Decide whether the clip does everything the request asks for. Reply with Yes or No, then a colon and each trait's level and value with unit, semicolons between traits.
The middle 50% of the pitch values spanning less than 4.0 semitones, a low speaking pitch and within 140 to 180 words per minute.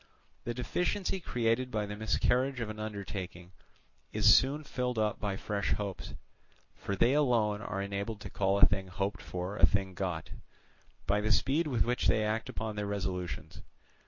Yes: average, 3.5 semitones; low, 105 Hz; average, 170 wpm